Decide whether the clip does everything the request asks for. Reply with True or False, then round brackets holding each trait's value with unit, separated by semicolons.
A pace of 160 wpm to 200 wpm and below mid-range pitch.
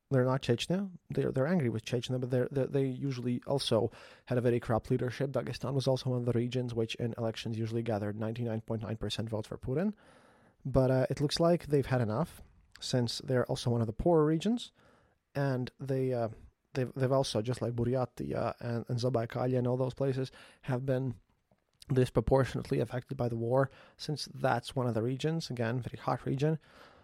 True (190 wpm; 125 Hz)